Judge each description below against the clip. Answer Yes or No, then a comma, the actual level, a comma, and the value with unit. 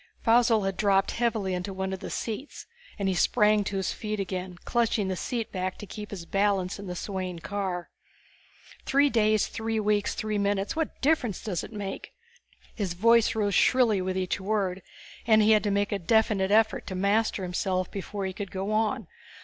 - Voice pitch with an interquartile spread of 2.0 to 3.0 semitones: Yes, narrow, 2.4 semitones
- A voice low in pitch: No, high, 205 Hz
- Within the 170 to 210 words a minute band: Yes, average, 190 wpm